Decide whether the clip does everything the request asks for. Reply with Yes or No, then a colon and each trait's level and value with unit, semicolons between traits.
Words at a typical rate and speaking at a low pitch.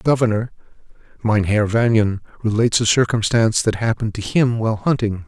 Yes: average, 150 wpm; low, 110 Hz